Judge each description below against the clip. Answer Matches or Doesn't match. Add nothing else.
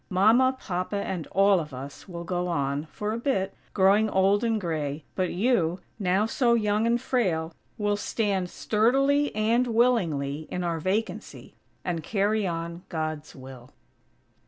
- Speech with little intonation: Doesn't match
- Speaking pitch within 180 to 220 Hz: Matches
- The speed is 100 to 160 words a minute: Matches